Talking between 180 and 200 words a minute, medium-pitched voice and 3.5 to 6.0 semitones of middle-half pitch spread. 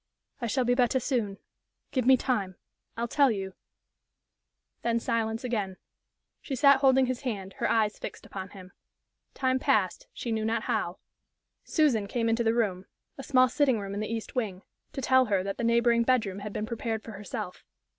No: average, 185 wpm; high, 230 Hz; average, 3.8 semitones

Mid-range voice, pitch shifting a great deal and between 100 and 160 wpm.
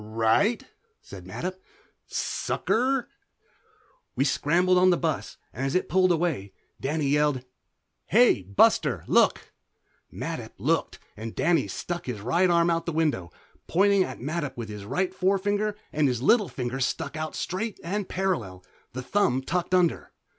Yes: medium, 165 Hz; wide, 6.0 semitones; average, 145 wpm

